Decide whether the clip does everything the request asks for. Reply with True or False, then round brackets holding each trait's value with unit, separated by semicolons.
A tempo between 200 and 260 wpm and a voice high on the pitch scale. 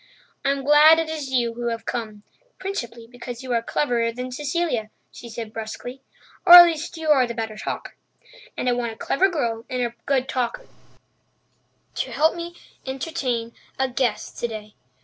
False (170 wpm; 250 Hz)